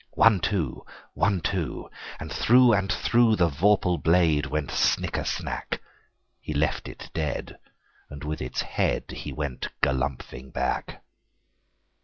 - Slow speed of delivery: Yes, slow, 115 wpm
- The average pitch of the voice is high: No, very low, 80 Hz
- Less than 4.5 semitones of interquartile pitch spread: No, wide, 5.5 semitones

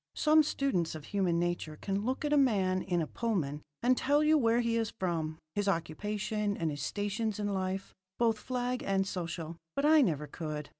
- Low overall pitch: No, high, 200 Hz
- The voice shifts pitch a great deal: Yes, wide, 5.7 semitones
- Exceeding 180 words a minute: Yes, average, 195 wpm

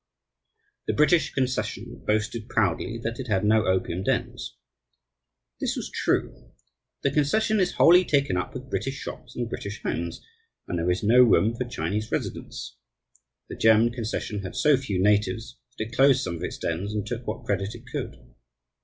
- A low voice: Yes, low, 110 Hz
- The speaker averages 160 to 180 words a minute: Yes, average, 170 wpm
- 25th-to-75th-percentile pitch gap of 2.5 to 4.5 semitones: No, average, 4.9 semitones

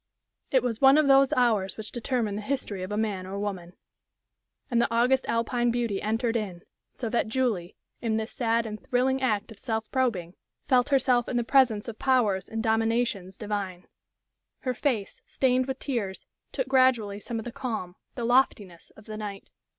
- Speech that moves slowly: No, average, 180 wpm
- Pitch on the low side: No, high, 230 Hz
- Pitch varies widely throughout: No, average, 3.4 semitones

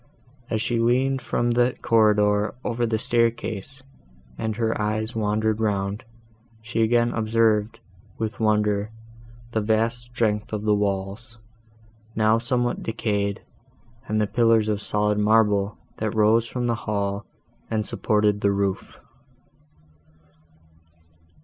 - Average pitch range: No, narrow, 1.7 semitones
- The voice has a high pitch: No, low, 110 Hz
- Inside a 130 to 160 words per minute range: No, slow, 120 wpm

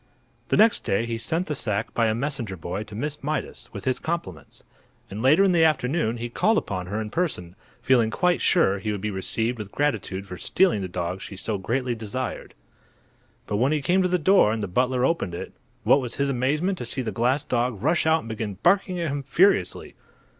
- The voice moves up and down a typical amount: No, wide, 6.8 semitones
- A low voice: Yes, low, 125 Hz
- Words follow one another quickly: Yes, fast, 220 wpm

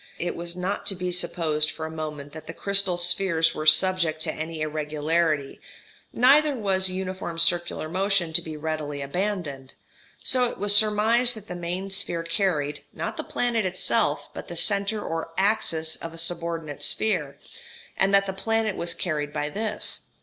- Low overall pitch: No, medium, 175 Hz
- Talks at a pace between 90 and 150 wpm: No, average, 170 wpm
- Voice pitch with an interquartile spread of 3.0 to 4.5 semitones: Yes, average, 4.0 semitones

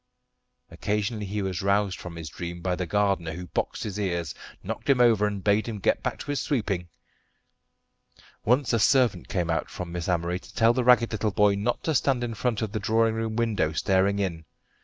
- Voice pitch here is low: Yes, low, 105 Hz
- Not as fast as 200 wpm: No, fast, 205 wpm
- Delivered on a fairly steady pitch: No, average, 4.0 semitones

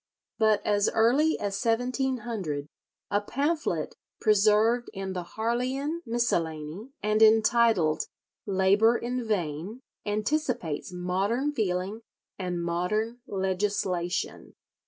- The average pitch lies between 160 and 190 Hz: No, high, 215 Hz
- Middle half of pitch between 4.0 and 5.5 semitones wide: Yes, average, 4.4 semitones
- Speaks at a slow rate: Yes, slow, 95 wpm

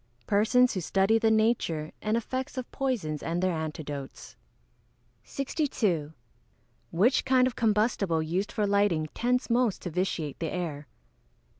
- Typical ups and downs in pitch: No, wide, 6.6 semitones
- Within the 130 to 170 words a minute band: Yes, average, 140 wpm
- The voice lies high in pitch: Yes, high, 200 Hz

